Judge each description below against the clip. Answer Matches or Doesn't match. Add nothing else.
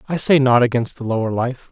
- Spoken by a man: Matches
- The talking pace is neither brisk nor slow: Doesn't match